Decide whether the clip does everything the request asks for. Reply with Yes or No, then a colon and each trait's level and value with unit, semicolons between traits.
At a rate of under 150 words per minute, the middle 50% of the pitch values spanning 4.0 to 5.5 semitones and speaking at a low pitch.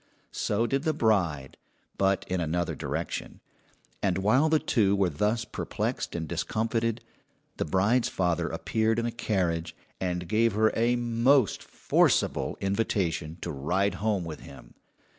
Yes: average, 140 wpm; average, 4.6 semitones; low, 100 Hz